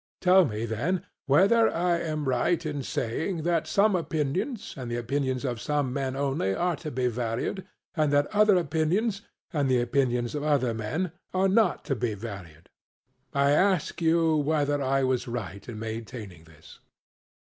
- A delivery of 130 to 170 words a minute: Yes, average, 165 wpm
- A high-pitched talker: No, medium, 140 Hz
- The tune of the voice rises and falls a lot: Yes, wide, 5.8 semitones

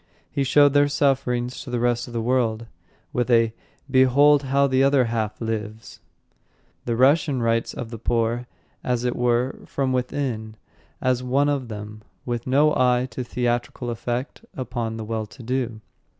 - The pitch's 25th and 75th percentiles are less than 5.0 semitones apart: Yes, narrow, 2.4 semitones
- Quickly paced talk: No, average, 165 wpm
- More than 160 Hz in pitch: No, low, 125 Hz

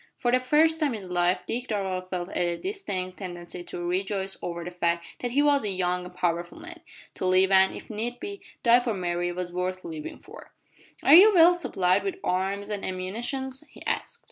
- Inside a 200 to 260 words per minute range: Yes, fast, 205 wpm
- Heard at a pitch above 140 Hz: Yes, high, 190 Hz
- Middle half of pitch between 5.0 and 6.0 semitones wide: Yes, wide, 5.4 semitones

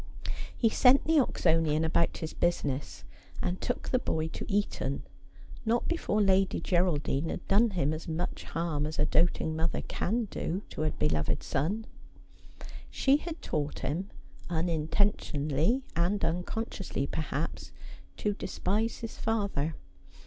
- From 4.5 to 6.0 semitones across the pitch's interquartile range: Yes, average, 5.2 semitones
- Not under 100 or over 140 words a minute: Yes, slow, 135 wpm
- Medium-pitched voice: Yes, medium, 175 Hz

